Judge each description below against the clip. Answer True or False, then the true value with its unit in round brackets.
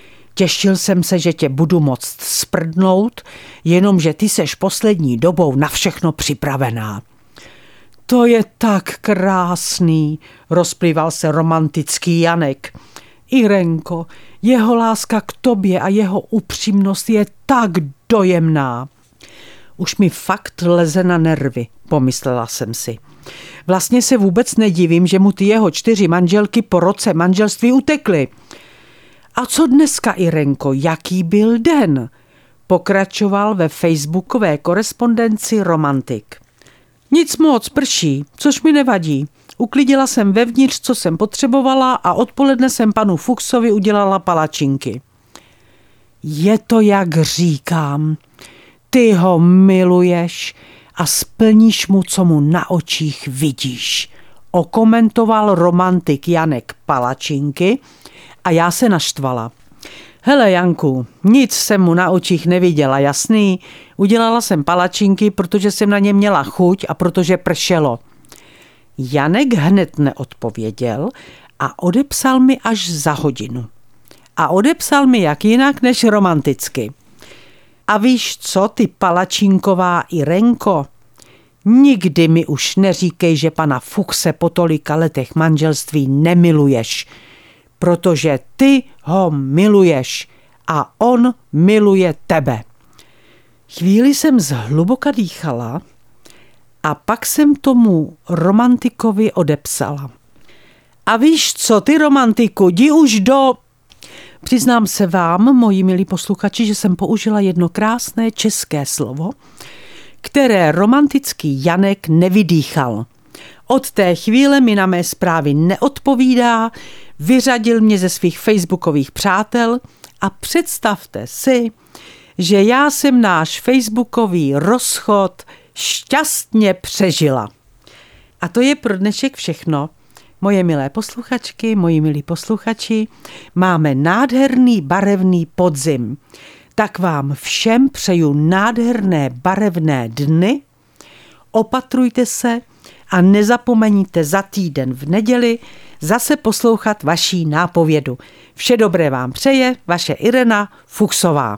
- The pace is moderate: False (110 wpm)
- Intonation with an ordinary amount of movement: False (6.3 semitones)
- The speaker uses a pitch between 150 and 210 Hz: True (185 Hz)